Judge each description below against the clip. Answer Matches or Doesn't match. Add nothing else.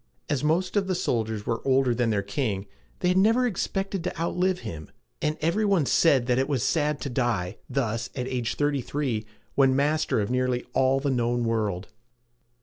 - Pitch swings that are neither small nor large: Doesn't match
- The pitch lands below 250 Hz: Matches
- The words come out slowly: Doesn't match